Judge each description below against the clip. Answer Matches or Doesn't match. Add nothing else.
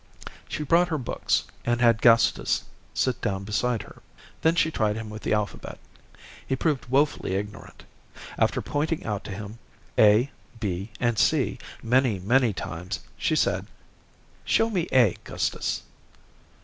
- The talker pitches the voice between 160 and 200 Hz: Doesn't match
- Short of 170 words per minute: Matches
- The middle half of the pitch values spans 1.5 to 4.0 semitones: Doesn't match